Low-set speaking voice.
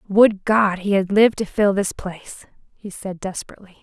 No: high, 195 Hz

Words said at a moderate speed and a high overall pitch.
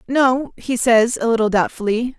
Yes: average, 165 wpm; high, 235 Hz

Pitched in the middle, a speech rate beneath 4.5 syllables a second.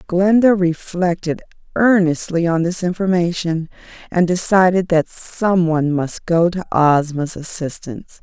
Yes: medium, 175 Hz; 4.3 syllables/s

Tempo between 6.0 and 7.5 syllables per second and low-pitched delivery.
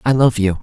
No: 5.7 syllables/s; low, 115 Hz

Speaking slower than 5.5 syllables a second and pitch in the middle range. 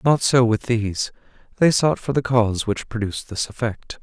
No: 5.2 syllables/s; low, 115 Hz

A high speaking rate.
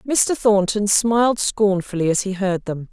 No: average, 165 wpm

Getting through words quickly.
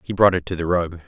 Yes: fast, 335 wpm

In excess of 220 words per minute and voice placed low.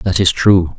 Yes: fast, 230 wpm; very low, 95 Hz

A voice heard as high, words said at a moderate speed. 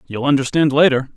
No: medium, 140 Hz; average, 155 wpm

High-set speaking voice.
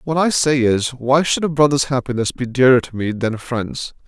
No: low, 130 Hz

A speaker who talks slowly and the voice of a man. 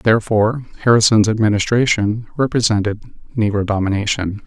Yes: slow, 80 wpm; male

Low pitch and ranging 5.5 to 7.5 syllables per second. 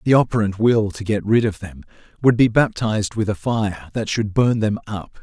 No: low, 105 Hz; 5.0 syllables/s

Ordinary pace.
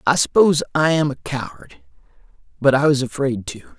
Yes: average, 175 wpm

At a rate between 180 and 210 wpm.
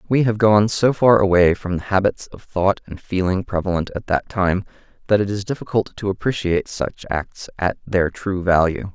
Yes: average, 195 wpm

